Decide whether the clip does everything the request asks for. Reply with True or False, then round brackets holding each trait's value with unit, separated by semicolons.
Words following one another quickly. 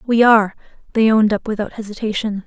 False (170 wpm)